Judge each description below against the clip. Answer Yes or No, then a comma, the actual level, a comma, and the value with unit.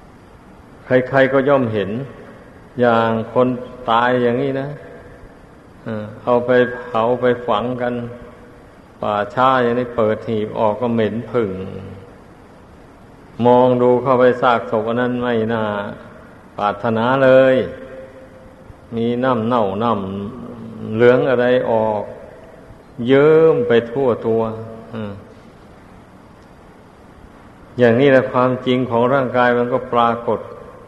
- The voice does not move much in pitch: Yes, narrow, 2.2 semitones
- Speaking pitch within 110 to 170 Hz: Yes, low, 120 Hz